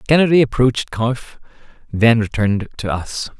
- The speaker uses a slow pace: Yes, slow, 125 wpm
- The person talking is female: No, male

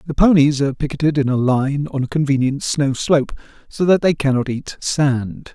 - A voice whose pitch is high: No, medium, 140 Hz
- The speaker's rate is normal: Yes, average, 195 wpm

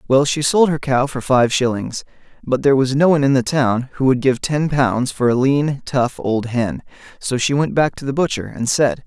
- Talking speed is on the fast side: Yes, fast, 240 wpm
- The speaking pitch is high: No, low, 130 Hz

